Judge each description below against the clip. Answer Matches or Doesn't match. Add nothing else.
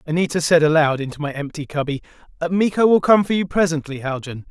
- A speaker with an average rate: Matches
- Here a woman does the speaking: Doesn't match